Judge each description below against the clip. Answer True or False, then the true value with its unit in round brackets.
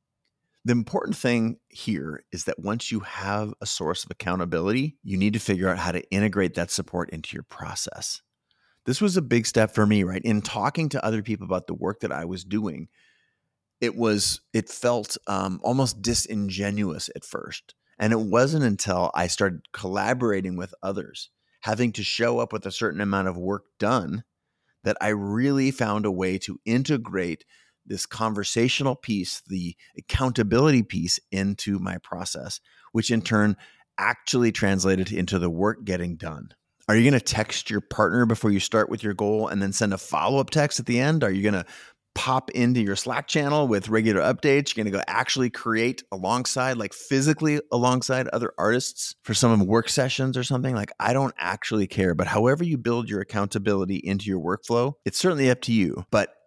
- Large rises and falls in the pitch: False (3.9 semitones)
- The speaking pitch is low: True (110 Hz)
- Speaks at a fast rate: False (185 wpm)